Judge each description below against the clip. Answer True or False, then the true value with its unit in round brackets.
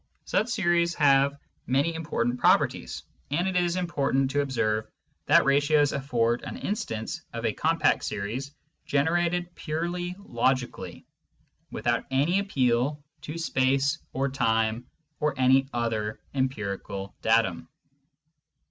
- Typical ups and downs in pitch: False (5.7 semitones)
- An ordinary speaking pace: False (115 wpm)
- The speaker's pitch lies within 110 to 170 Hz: True (135 Hz)